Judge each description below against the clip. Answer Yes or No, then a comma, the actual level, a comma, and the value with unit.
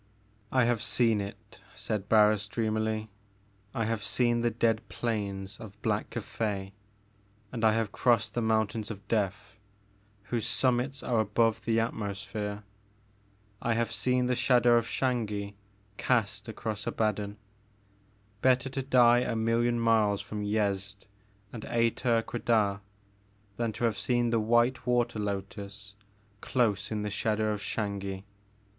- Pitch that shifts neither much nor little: No, narrow, 2.3 semitones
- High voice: No, low, 110 Hz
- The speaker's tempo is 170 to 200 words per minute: No, average, 140 wpm